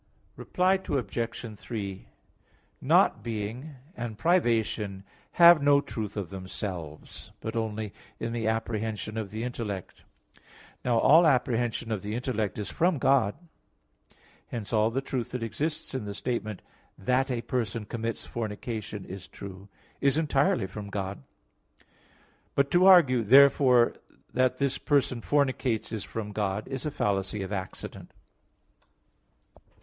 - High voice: No, low, 115 Hz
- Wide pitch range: No, average, 4.2 semitones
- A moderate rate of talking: No, slow, 130 wpm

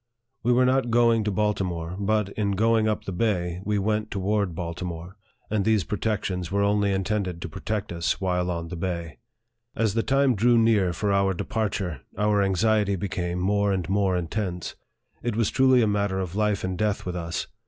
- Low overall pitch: Yes, low, 100 Hz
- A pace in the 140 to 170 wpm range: No, average, 185 wpm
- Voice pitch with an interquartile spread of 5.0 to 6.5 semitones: No, average, 3.0 semitones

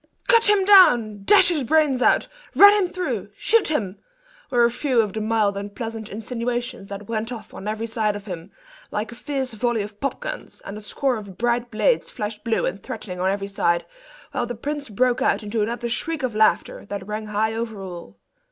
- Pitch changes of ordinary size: Yes, average, 3.6 semitones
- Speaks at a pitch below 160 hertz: No, high, 225 Hz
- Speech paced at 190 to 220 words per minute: Yes, fast, 205 wpm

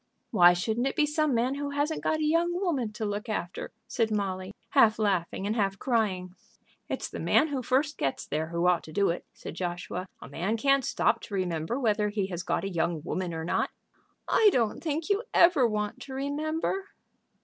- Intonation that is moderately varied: No, wide, 7.5 semitones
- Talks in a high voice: Yes, high, 220 Hz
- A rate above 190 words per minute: Yes, fast, 205 wpm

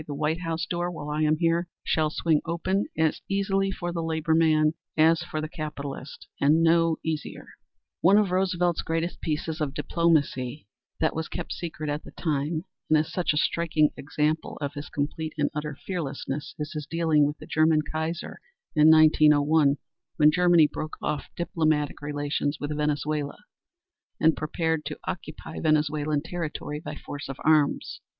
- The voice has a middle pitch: Yes, medium, 155 Hz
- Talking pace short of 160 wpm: No, average, 165 wpm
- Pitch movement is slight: Yes, narrow, 1.8 semitones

